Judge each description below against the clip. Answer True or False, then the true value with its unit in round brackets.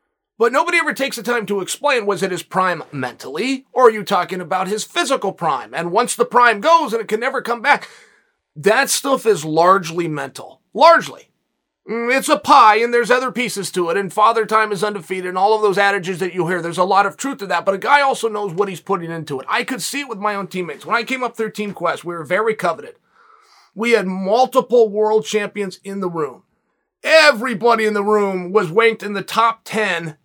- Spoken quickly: True (225 wpm)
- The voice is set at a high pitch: True (215 Hz)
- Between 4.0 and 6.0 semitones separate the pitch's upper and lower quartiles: True (4.6 semitones)